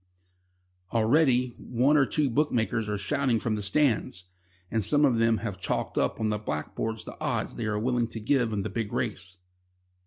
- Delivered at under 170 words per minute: No, average, 180 wpm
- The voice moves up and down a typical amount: Yes, average, 3.1 semitones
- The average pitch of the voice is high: No, low, 115 Hz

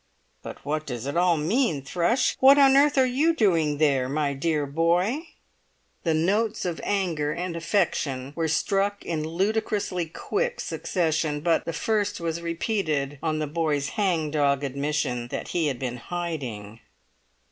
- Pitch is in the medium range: Yes, medium, 165 Hz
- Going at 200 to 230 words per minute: No, average, 155 wpm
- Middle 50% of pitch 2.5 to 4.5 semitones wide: No, average, 5.3 semitones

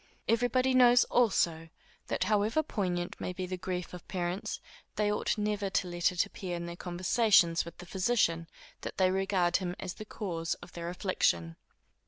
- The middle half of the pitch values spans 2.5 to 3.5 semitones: Yes, average, 3.2 semitones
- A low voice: No, medium, 185 Hz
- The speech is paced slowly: No, average, 180 wpm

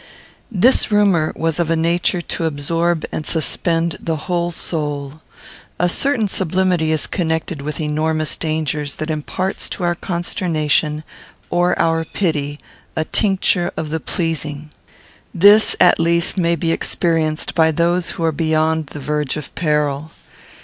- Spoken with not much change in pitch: Yes, narrow, 2.1 semitones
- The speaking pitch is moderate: Yes, medium, 165 Hz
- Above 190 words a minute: No, average, 140 wpm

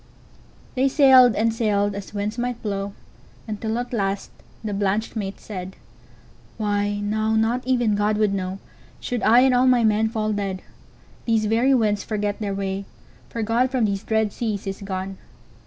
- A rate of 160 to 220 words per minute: No, average, 150 wpm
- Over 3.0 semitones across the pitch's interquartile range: No, narrow, 2.4 semitones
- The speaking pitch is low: No, high, 215 Hz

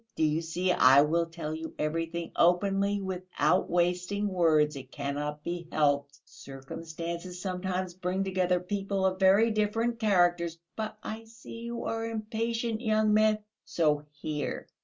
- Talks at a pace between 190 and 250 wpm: No, average, 140 wpm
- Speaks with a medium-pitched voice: Yes, medium, 180 Hz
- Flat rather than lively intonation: No, average, 4.4 semitones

